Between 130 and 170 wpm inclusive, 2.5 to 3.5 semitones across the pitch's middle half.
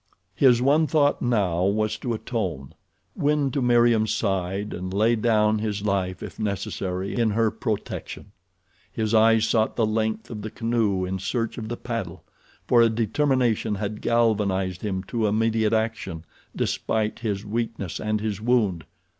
Yes: average, 150 wpm; average, 2.8 semitones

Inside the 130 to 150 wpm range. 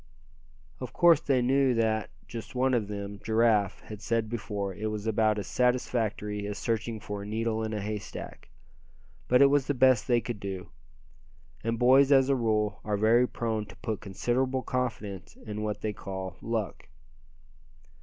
No: average, 175 wpm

